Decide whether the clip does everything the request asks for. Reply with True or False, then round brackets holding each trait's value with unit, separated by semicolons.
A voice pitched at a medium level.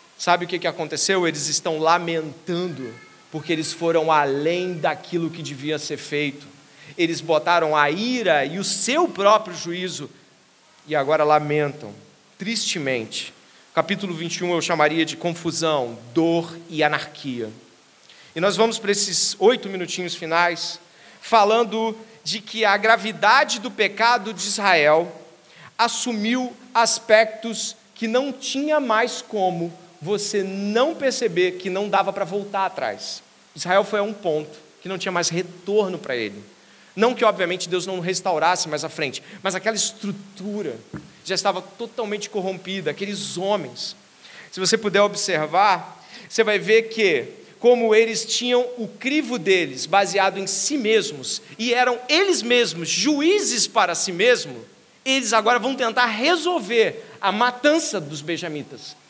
False (195 Hz)